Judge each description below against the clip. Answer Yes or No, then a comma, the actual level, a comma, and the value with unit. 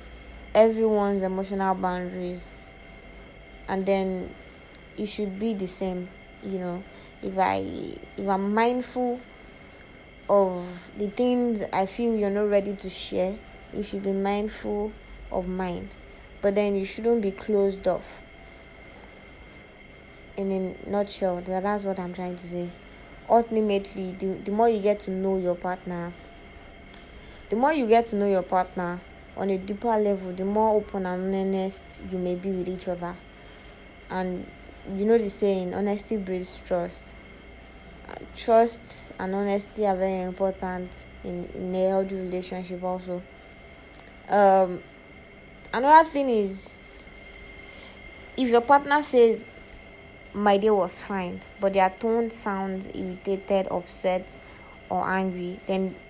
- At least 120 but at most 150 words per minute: Yes, slow, 135 wpm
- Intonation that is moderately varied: No, narrow, 2.2 semitones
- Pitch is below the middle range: No, high, 190 Hz